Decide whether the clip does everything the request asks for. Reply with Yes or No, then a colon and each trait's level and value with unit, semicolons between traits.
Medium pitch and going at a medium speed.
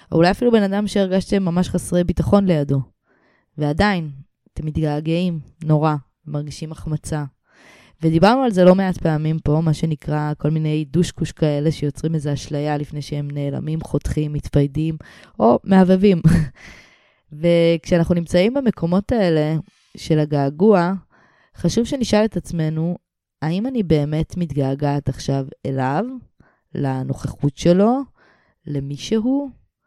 Yes: medium, 160 Hz; average, 120 wpm